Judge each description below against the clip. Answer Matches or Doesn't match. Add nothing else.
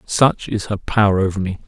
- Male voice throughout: Matches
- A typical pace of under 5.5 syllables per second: Matches